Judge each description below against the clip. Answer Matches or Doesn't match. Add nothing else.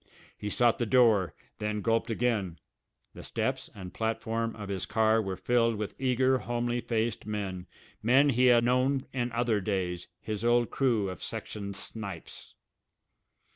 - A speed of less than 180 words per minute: Matches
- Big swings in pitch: Doesn't match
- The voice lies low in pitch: Matches